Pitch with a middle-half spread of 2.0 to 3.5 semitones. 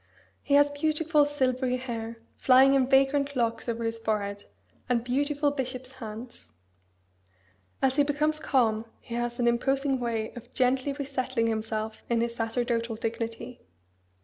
Yes: average, 3.1 semitones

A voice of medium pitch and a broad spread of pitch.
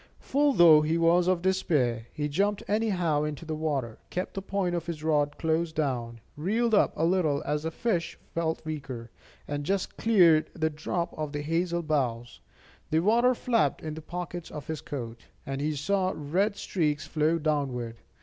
No: medium, 160 Hz; average, 3.5 semitones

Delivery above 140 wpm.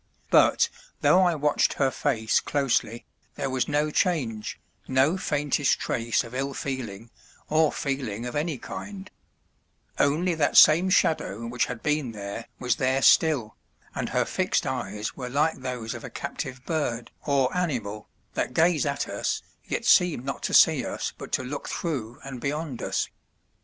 Yes: average, 160 wpm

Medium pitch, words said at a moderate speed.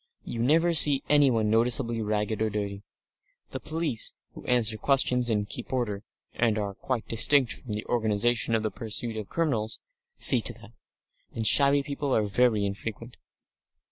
No: low, 115 Hz; average, 160 wpm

